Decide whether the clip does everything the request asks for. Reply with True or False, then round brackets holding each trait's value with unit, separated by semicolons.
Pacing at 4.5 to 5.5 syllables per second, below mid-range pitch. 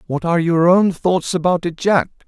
False (5.1 syllables/s; 175 Hz)